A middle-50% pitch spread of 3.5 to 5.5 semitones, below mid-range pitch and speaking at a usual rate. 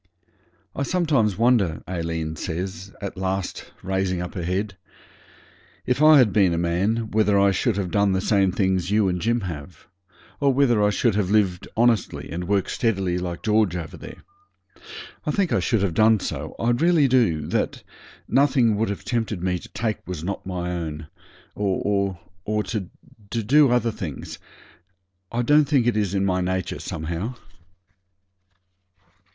Yes: average, 4.2 semitones; low, 100 Hz; average, 165 wpm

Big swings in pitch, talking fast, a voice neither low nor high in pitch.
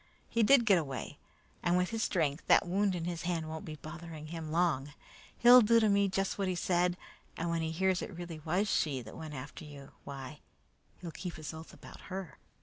No: average, 3.4 semitones; fast, 215 wpm; medium, 170 Hz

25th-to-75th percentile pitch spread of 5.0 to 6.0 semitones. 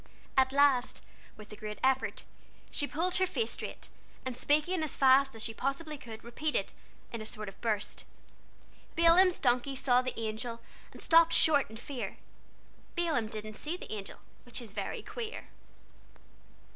Yes: wide, 5.5 semitones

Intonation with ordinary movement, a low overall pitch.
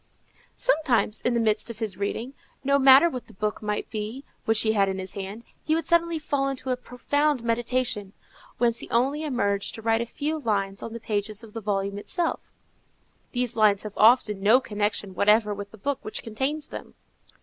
No: average, 4.2 semitones; high, 225 Hz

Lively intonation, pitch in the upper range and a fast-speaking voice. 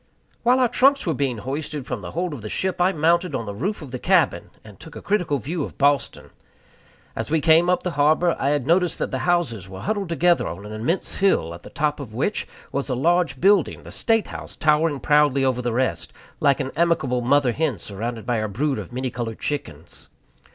No: wide, 5.8 semitones; medium, 145 Hz; fast, 220 wpm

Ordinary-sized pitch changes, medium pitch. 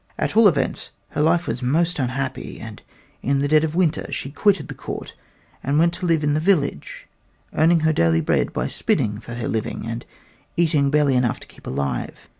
Yes: average, 4.9 semitones; medium, 145 Hz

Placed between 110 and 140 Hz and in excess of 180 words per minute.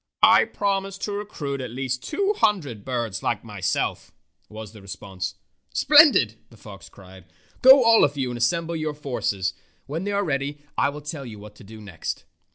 Yes: low, 135 Hz; average, 195 wpm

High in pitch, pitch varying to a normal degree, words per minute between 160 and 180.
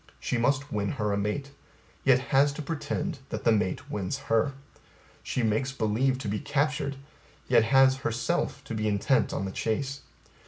No: low, 130 Hz; average, 4.5 semitones; average, 170 wpm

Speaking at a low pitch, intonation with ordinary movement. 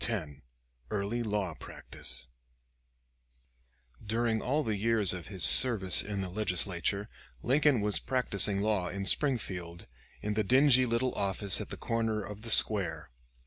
Yes: low, 105 Hz; average, 3.2 semitones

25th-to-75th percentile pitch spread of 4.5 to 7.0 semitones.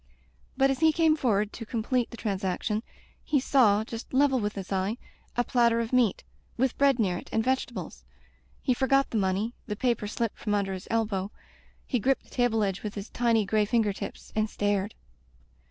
No: average, 3.6 semitones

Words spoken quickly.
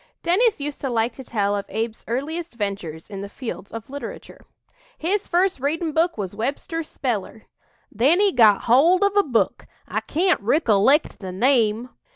No: average, 175 wpm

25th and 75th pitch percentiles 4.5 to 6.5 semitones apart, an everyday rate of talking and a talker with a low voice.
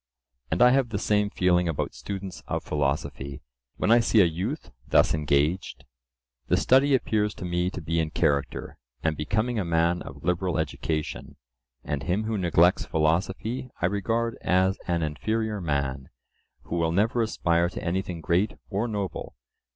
Yes: average, 5.1 semitones; average, 160 wpm; very low, 90 Hz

